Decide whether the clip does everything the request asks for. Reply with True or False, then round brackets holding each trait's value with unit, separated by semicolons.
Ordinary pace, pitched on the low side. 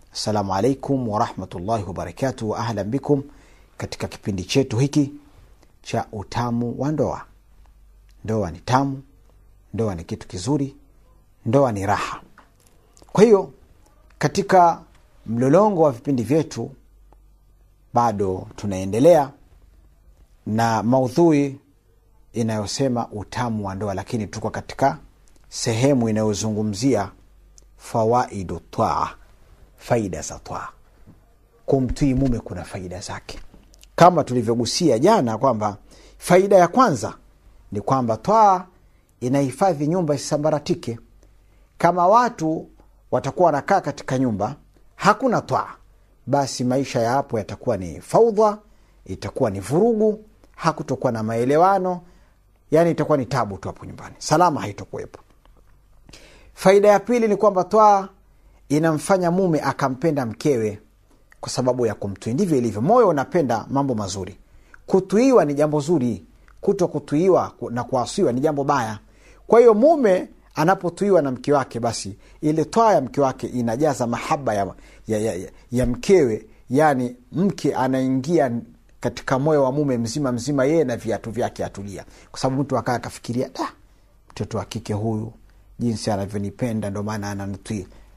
True (110 wpm; 120 Hz)